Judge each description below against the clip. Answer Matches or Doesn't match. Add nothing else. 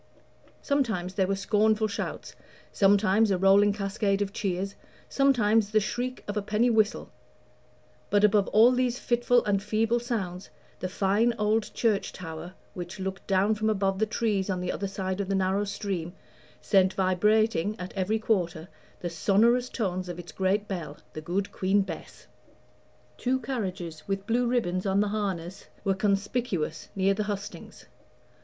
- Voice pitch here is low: Doesn't match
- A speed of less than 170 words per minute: Matches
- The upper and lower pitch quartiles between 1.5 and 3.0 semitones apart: Matches